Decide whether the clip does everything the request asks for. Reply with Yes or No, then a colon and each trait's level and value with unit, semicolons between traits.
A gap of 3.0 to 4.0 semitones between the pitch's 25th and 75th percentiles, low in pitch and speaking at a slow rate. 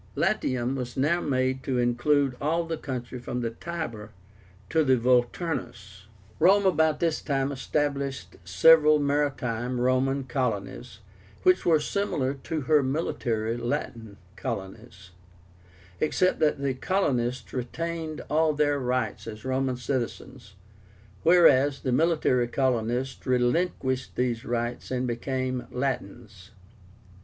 Yes: average, 3.7 semitones; low, 130 Hz; slow, 115 wpm